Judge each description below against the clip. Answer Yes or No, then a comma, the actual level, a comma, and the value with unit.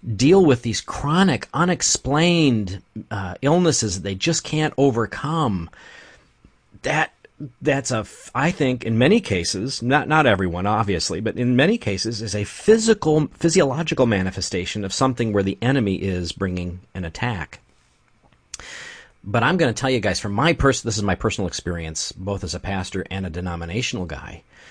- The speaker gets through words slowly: No, average, 165 wpm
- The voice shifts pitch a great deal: Yes, wide, 6.6 semitones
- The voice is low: Yes, low, 115 Hz